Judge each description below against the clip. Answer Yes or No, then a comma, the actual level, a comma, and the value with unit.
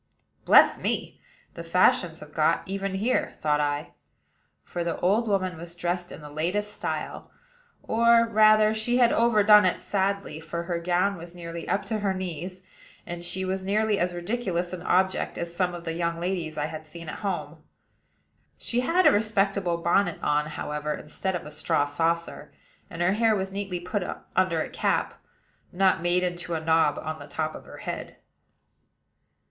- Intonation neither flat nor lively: Yes, average, 3.1 semitones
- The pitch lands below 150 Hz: No, medium, 180 Hz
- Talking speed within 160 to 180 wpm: Yes, average, 175 wpm